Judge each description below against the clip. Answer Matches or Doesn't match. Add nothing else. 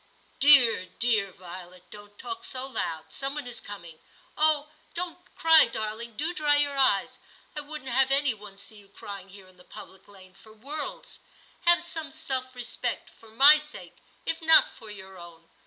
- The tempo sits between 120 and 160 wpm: Doesn't match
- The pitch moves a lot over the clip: Matches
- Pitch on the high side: Matches